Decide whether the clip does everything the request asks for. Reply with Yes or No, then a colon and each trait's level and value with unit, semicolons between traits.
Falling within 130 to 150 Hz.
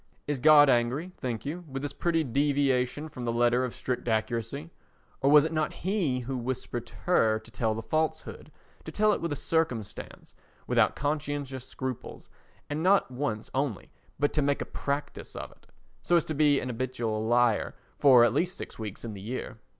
Yes: low, 135 Hz